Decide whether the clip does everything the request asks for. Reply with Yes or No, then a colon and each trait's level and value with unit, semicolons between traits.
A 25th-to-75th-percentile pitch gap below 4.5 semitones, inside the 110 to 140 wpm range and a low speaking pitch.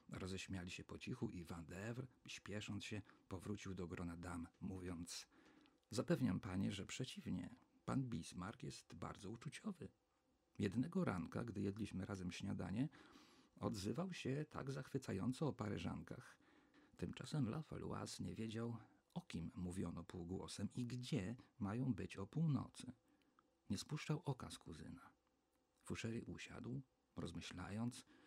No: wide, 5.6 semitones; average, 120 wpm; low, 105 Hz